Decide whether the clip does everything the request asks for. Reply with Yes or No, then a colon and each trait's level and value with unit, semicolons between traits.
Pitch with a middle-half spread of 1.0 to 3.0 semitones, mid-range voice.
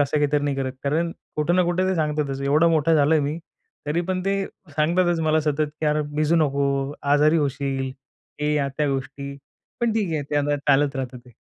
Yes: narrow, 2.5 semitones; medium, 150 Hz